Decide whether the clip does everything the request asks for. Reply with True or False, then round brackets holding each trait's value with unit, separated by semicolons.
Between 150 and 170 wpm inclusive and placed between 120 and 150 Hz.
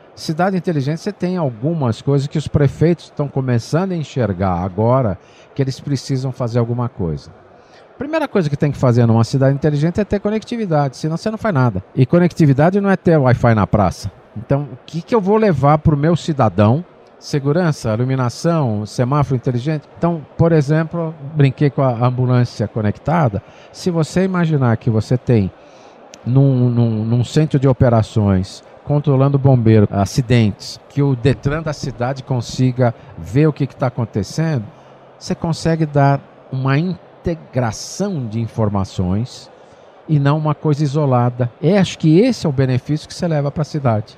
True (165 wpm; 140 Hz)